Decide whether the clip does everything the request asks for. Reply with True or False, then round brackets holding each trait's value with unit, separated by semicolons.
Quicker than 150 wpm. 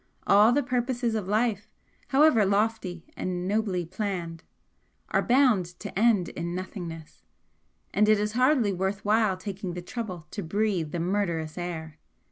False (145 wpm)